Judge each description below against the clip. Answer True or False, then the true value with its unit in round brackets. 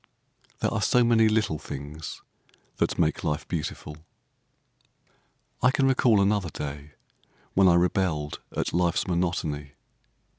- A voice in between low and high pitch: False (85 Hz)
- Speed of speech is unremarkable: False (120 wpm)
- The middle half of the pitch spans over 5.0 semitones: True (5.5 semitones)